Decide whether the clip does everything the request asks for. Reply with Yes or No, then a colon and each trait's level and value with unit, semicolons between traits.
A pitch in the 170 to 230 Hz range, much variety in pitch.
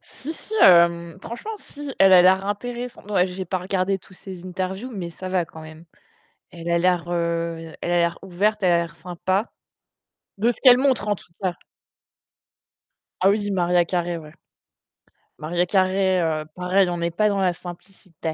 No: medium, 185 Hz; narrow, 2.5 semitones